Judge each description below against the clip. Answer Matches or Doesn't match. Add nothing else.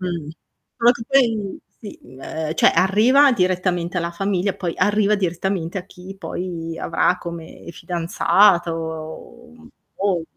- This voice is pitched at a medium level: Matches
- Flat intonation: Doesn't match